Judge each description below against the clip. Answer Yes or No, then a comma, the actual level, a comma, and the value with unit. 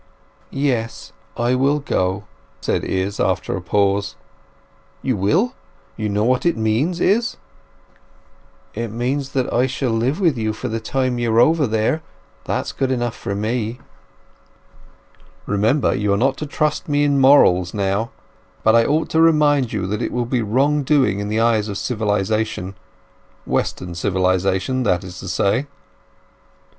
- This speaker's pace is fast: No, average, 150 wpm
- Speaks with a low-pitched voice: Yes, low, 115 Hz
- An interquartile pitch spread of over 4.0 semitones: Yes, average, 4.9 semitones